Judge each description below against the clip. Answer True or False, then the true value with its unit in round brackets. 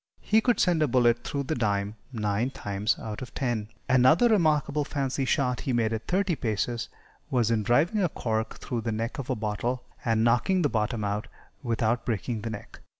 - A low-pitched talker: True (120 Hz)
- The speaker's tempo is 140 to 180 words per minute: False (195 wpm)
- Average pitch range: True (4.1 semitones)